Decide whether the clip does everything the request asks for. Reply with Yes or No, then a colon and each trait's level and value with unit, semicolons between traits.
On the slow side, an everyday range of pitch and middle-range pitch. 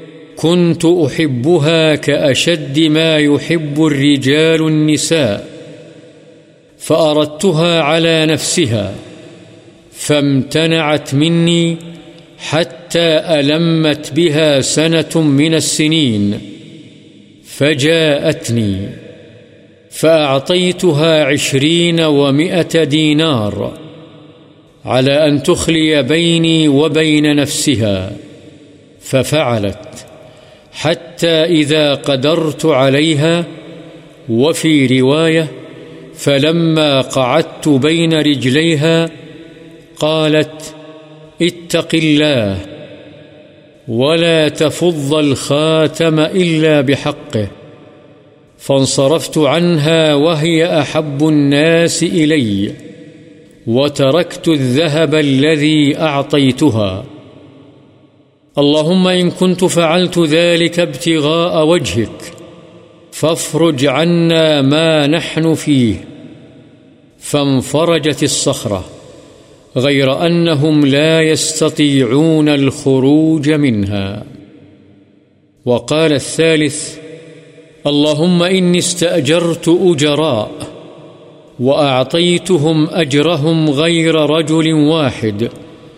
No: slow, 60 wpm; narrow, 1.9 semitones; medium, 155 Hz